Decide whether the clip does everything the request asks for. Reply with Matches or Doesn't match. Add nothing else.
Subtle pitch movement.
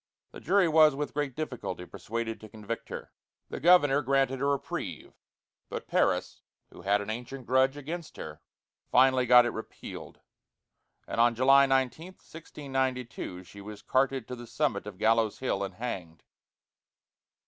Doesn't match